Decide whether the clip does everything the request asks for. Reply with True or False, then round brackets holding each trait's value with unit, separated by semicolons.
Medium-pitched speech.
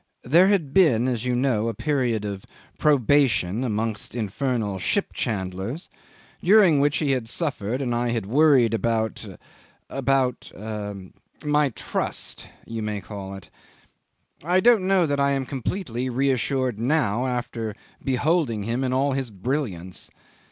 False (125 Hz)